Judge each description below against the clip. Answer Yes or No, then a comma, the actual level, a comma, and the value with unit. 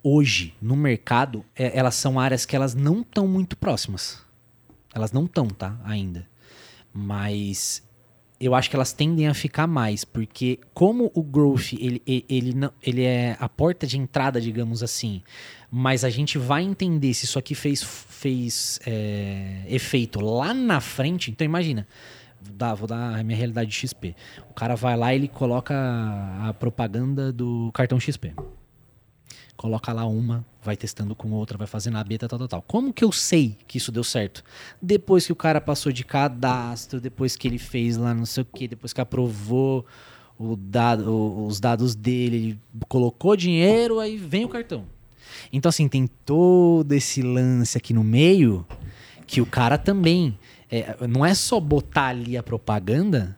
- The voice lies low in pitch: Yes, low, 125 Hz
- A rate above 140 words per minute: Yes, average, 170 wpm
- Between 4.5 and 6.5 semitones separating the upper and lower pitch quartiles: No, average, 3.8 semitones